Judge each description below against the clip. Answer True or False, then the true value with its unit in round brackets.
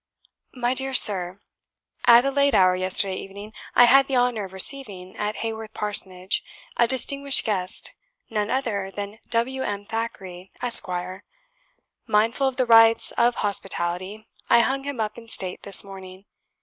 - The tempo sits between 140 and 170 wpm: True (150 wpm)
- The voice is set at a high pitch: True (215 Hz)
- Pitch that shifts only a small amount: False (4.2 semitones)